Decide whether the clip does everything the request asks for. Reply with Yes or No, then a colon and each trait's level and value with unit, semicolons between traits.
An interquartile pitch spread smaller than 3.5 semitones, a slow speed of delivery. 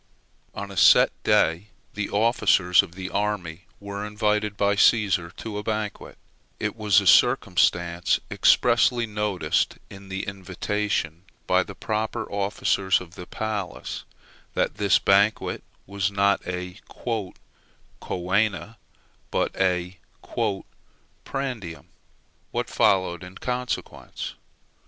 Yes: average, 2.7 semitones; slow, 110 wpm